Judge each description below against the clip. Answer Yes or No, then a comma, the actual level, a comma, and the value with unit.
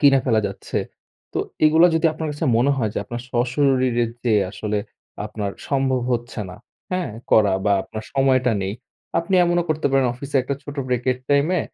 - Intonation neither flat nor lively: Yes, average, 3.7 semitones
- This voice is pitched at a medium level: No, low, 130 Hz